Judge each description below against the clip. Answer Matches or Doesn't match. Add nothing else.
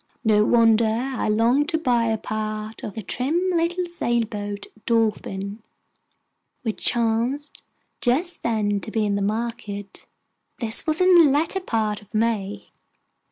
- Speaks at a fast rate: Doesn't match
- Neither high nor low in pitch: Doesn't match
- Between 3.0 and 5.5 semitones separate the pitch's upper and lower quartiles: Matches